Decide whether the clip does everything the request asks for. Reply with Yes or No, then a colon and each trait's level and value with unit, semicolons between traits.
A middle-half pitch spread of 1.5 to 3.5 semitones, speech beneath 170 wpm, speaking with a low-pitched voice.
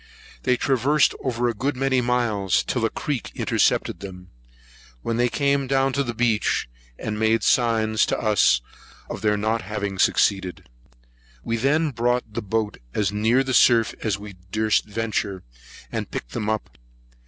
Yes: average, 3.1 semitones; average, 160 wpm; low, 115 Hz